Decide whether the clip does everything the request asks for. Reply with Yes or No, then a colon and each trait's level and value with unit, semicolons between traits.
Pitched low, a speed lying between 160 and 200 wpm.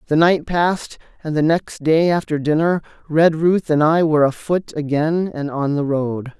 No: medium, 155 Hz; average, 180 wpm